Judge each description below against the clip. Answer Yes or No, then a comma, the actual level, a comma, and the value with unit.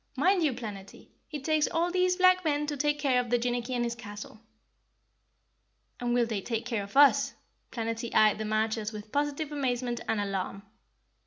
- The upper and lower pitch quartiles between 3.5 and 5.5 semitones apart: Yes, average, 5.1 semitones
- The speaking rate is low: No, average, 175 wpm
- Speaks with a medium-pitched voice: No, high, 245 Hz